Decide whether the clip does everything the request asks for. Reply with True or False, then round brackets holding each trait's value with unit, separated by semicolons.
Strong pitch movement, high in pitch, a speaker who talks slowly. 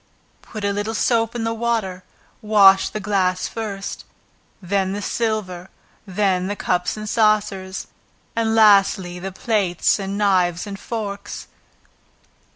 False (2.4 semitones; 200 Hz; 130 wpm)